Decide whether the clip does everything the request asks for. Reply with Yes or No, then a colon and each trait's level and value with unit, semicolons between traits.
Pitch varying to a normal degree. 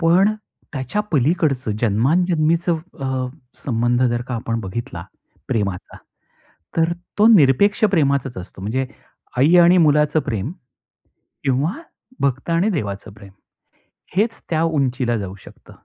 No: wide, 6.0 semitones